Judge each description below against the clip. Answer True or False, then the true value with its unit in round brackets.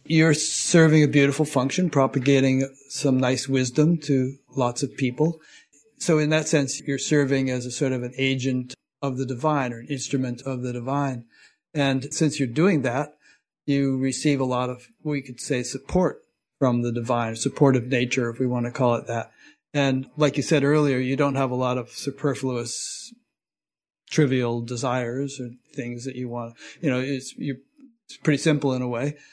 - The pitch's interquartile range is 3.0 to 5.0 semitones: False (2.6 semitones)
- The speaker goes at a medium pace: True (180 wpm)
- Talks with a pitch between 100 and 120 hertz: False (135 Hz)